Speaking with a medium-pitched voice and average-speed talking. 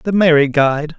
Yes: medium, 155 Hz; average, 185 wpm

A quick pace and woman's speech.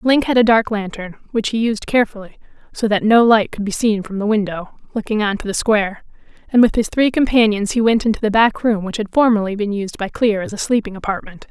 Yes: fast, 240 wpm; female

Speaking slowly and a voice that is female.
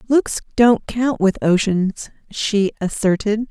Yes: slow, 120 wpm; female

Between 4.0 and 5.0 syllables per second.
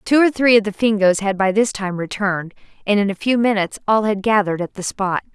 No: 6.1 syllables/s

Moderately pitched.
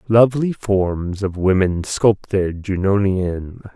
No: low, 100 Hz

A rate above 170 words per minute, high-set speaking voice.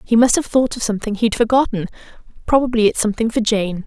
Yes: average, 200 wpm; high, 225 Hz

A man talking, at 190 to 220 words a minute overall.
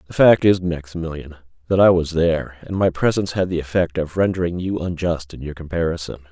Yes: male; average, 200 wpm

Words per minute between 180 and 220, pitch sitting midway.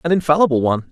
Yes: average, 200 wpm; medium, 145 Hz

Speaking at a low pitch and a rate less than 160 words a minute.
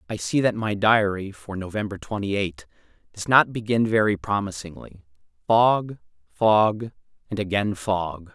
Yes: low, 100 Hz; slow, 135 wpm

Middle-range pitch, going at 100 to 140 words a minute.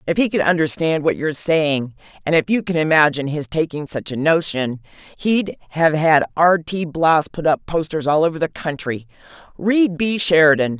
No: medium, 160 Hz; average, 180 wpm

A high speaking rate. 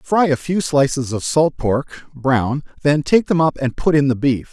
Yes: fast, 225 wpm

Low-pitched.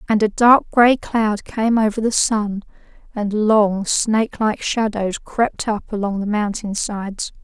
No: high, 215 Hz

